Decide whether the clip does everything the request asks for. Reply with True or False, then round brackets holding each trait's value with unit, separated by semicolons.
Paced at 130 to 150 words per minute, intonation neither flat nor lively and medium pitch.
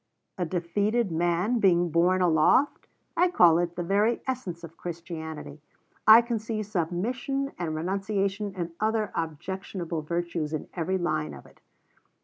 True (140 wpm; 4.1 semitones; 180 Hz)